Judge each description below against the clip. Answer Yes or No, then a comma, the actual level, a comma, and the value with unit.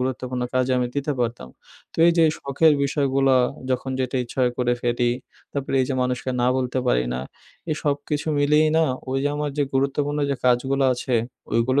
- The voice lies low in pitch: Yes, low, 130 Hz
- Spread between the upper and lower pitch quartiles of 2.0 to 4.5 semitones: Yes, narrow, 2.4 semitones